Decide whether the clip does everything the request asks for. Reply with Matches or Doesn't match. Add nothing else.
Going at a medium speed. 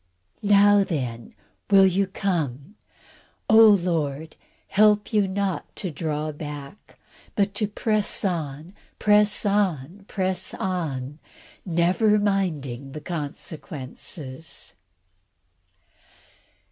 Doesn't match